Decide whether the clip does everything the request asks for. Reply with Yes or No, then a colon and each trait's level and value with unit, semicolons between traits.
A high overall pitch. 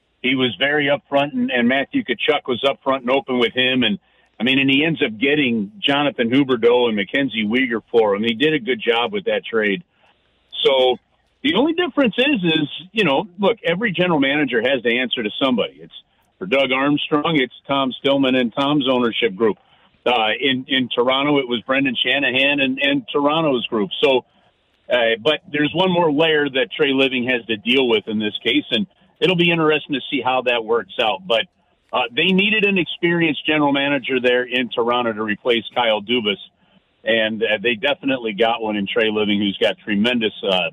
No: medium, 140 Hz